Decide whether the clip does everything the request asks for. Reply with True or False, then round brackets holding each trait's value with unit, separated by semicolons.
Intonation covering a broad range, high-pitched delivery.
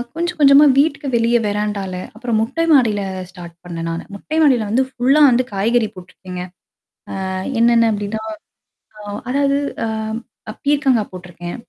True (5.9 semitones; 230 Hz)